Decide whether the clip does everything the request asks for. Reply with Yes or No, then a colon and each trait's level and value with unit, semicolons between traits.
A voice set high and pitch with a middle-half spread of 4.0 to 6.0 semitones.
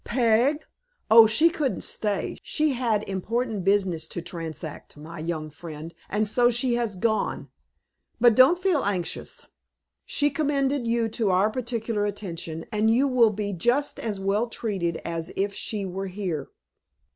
Yes: high, 215 Hz; average, 4.8 semitones